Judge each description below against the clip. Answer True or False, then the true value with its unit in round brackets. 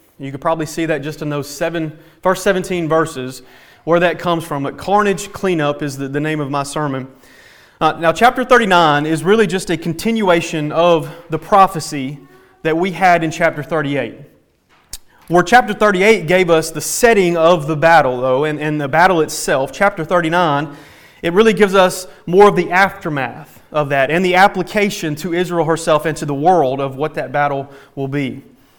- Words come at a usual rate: True (185 wpm)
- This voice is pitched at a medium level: True (165 Hz)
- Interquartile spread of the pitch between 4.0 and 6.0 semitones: False (3.6 semitones)